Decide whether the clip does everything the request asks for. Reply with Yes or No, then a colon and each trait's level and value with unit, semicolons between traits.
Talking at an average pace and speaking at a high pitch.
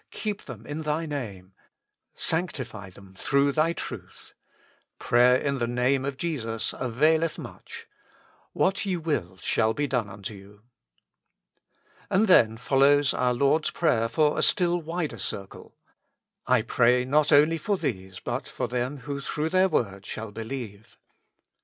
No: average, 155 wpm; low, 135 Hz